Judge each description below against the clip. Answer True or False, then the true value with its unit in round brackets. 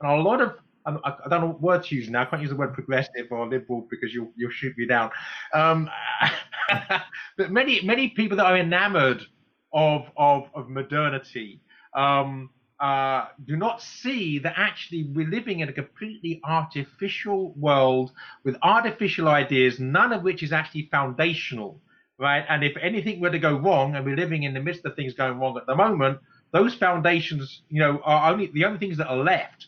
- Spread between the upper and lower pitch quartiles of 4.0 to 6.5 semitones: True (4.7 semitones)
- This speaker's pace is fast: False (190 wpm)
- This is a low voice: False (150 Hz)